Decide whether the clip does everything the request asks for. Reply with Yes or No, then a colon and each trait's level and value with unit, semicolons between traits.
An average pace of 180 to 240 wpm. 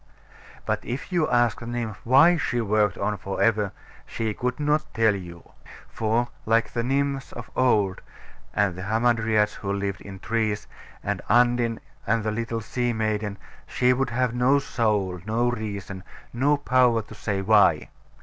No: average, 160 wpm